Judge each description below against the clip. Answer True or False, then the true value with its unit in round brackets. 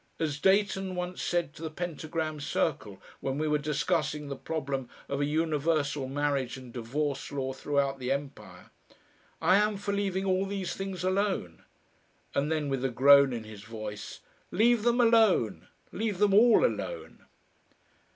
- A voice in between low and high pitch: True (150 Hz)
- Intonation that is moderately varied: False (5.8 semitones)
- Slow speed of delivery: False (155 wpm)